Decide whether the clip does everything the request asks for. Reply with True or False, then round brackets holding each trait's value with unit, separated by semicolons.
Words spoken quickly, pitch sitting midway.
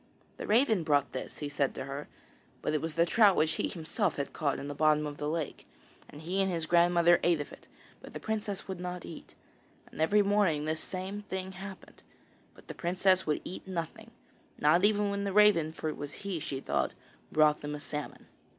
True (215 wpm; 170 Hz)